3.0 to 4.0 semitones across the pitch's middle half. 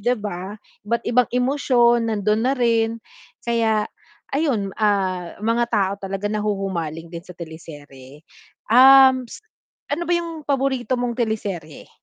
No: average, 4.4 semitones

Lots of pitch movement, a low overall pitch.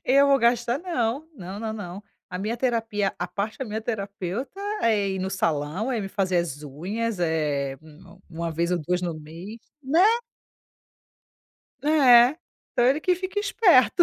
No: wide, 5.9 semitones; high, 205 Hz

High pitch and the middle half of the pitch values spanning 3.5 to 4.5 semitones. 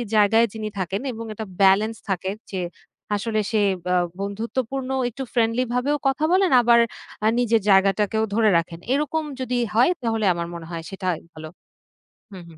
Yes: high, 220 Hz; average, 4.0 semitones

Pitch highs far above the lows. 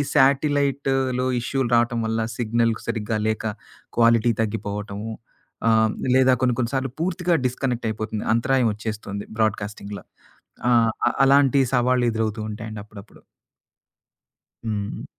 No: average, 3.3 semitones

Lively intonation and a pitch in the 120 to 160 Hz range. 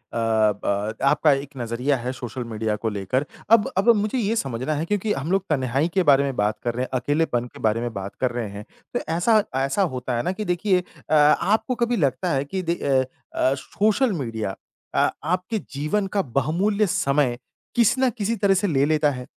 Yes: wide, 8.1 semitones; medium, 140 Hz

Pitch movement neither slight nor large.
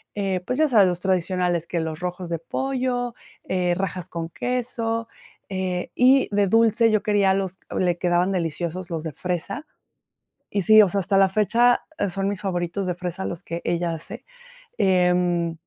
Yes: average, 3.1 semitones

